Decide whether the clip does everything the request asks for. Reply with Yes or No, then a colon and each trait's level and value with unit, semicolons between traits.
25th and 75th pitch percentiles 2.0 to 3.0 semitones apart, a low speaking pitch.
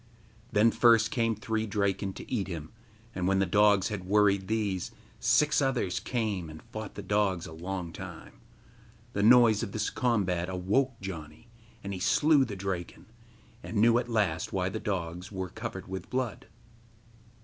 No: average, 3.4 semitones; low, 100 Hz